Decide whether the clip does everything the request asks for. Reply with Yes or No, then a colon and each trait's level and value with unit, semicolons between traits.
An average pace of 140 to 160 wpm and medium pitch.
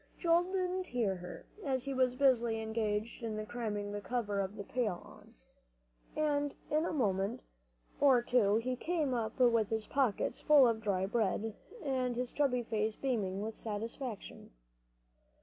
No: average, 150 wpm; high, 235 Hz